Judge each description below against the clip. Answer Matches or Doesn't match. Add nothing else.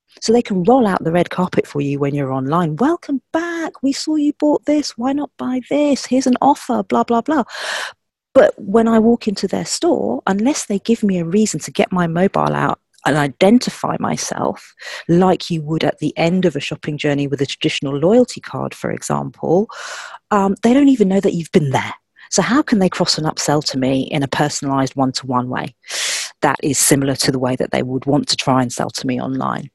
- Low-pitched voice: Doesn't match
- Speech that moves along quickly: Matches